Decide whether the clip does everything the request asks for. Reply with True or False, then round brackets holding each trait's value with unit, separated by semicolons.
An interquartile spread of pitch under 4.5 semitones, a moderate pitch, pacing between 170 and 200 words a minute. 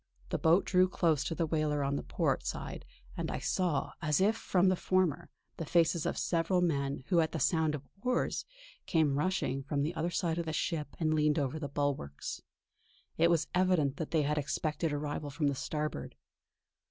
True (2.9 semitones; 155 Hz; 195 wpm)